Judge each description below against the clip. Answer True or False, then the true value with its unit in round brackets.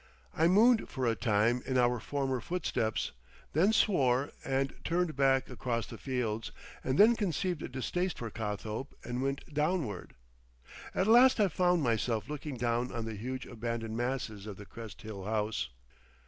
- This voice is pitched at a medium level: False (130 Hz)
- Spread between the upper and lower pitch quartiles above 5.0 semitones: True (5.4 semitones)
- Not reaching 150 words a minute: False (160 wpm)